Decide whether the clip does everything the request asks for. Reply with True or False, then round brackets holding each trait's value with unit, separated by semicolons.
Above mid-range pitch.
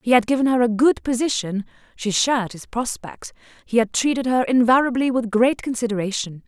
True (240 Hz)